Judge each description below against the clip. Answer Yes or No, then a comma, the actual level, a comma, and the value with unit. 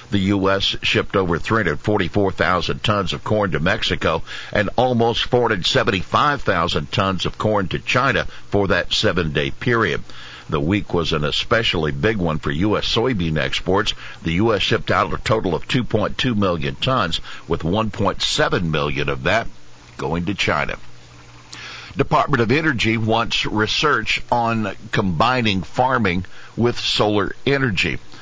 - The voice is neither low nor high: No, low, 100 Hz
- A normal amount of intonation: No, wide, 5.9 semitones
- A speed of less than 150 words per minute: Yes, slow, 135 wpm